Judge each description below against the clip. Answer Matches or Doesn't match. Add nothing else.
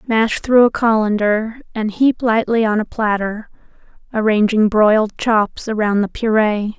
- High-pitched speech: Matches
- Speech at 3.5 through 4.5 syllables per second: Matches